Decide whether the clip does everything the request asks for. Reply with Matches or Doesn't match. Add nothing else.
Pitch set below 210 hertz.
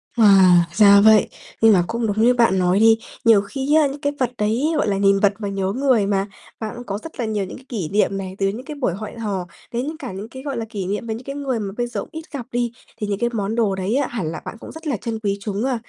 Doesn't match